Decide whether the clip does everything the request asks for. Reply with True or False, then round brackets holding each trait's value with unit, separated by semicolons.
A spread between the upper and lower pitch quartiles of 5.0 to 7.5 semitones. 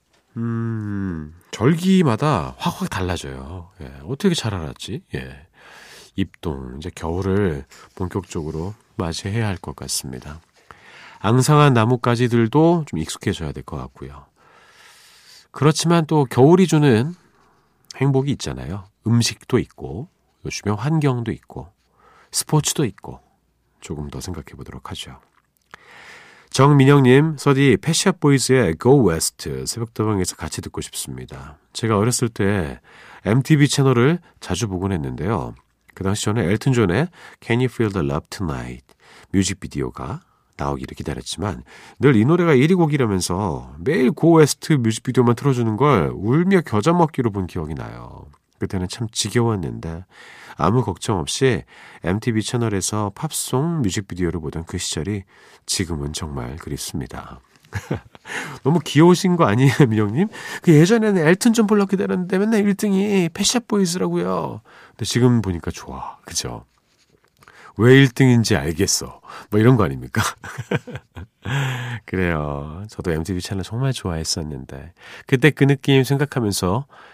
False (7.9 semitones)